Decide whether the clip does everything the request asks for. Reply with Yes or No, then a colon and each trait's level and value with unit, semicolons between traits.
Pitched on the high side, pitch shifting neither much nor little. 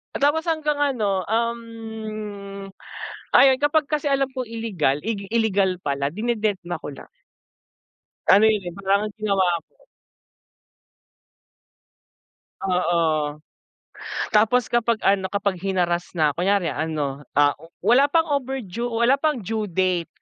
No: high, 205 Hz; wide, 5.8 semitones